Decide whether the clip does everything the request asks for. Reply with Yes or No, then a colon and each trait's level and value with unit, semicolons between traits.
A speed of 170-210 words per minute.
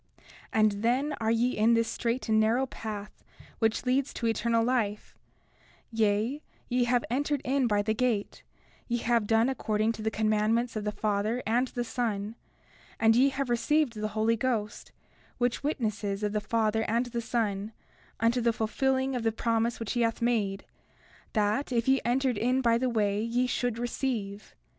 Yes: average, 175 wpm